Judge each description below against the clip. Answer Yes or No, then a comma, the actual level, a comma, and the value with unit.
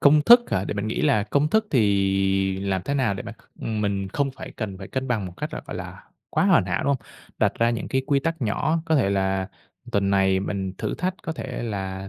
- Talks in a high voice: No, low, 105 Hz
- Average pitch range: No, wide, 6.1 semitones